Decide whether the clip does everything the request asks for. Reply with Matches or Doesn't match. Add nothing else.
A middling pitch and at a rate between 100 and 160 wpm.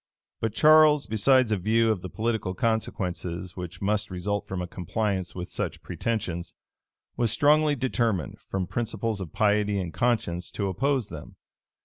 Doesn't match